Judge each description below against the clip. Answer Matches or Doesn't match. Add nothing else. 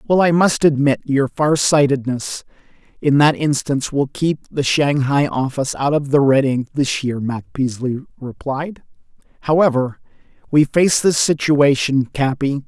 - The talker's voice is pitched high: Doesn't match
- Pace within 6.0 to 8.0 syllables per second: Doesn't match